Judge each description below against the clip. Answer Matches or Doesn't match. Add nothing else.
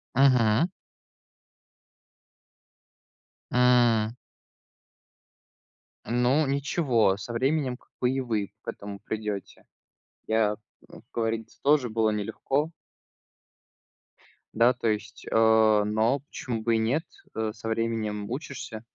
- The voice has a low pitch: Matches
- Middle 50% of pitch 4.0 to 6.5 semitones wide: Doesn't match